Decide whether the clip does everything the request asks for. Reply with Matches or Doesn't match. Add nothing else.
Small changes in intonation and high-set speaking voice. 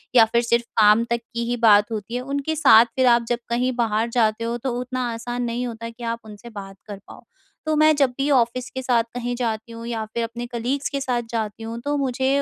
Matches